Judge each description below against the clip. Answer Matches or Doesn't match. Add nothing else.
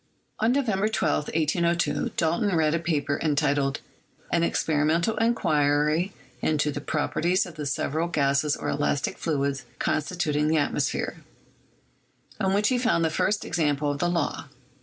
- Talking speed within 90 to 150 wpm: Matches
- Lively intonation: Doesn't match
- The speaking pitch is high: Doesn't match